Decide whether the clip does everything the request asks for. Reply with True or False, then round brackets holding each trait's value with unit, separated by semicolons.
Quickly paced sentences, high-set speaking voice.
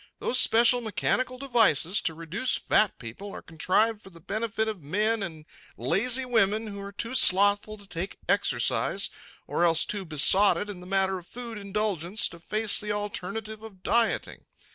False (165 wpm; 205 Hz)